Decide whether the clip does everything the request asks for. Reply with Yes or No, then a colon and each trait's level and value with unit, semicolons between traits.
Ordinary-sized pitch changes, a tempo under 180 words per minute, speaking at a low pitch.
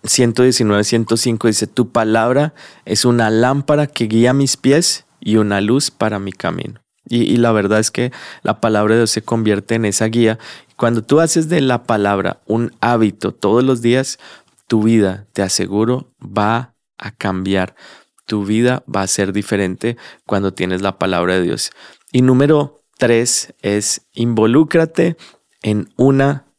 Yes: average, 3.5 semitones; average, 160 wpm; low, 115 Hz